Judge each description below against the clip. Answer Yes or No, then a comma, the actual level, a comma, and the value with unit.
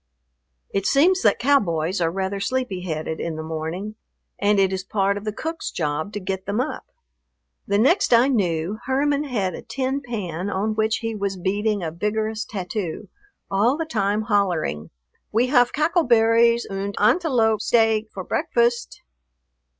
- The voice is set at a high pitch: Yes, high, 210 Hz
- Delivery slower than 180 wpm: Yes, average, 165 wpm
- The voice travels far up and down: No, average, 4.0 semitones